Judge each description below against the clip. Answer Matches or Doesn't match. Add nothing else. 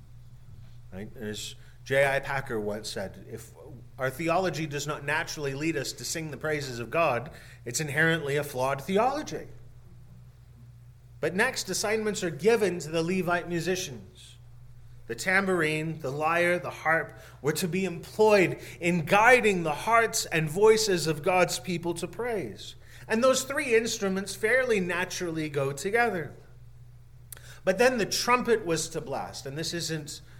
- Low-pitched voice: Doesn't match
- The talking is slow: Doesn't match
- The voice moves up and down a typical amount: Doesn't match